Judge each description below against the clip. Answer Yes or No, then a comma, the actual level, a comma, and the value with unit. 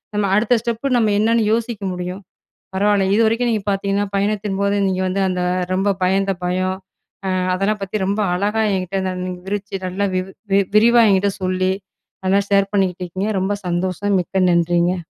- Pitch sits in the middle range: No, high, 195 Hz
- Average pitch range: No, narrow, 2.0 semitones